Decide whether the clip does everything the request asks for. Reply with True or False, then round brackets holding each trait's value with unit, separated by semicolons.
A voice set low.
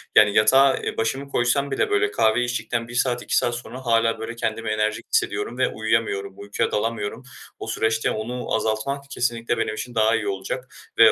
True (115 Hz)